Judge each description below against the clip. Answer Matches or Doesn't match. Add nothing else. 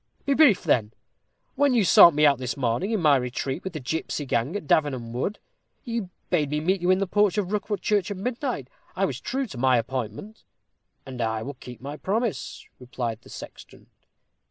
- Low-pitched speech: Doesn't match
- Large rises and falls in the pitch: Matches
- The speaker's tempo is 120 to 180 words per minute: Doesn't match